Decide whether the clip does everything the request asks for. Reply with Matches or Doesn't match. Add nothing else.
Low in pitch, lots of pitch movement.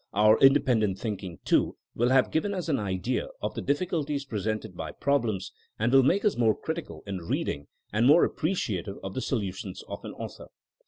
Matches